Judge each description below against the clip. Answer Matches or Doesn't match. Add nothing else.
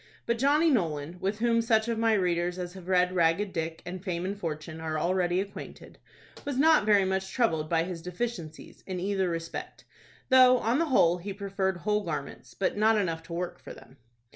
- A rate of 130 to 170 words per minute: Doesn't match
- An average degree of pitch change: Matches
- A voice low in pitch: Doesn't match